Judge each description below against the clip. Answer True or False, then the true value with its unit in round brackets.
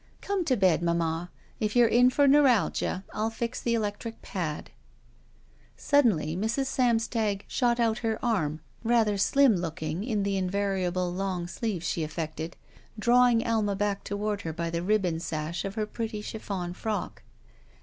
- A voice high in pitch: True (205 Hz)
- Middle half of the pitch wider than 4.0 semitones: True (4.6 semitones)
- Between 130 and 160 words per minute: True (155 wpm)